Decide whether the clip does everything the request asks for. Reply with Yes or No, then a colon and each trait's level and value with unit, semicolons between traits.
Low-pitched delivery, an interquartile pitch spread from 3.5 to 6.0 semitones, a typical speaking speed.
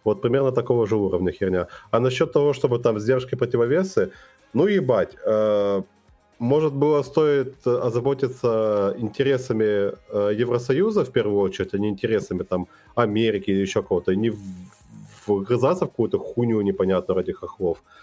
Yes: low, 115 Hz; average, 4.6 semitones; average, 145 wpm